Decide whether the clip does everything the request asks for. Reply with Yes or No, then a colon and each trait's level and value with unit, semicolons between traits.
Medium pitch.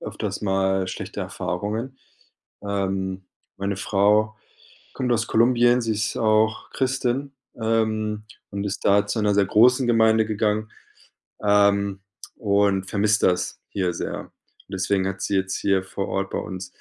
No: low, 105 Hz